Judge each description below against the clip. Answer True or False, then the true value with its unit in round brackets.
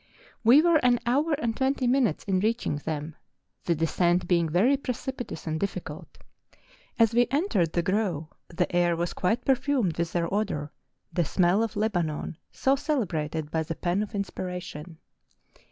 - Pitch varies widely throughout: True (6.5 semitones)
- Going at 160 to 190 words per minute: True (165 wpm)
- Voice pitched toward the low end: False (185 Hz)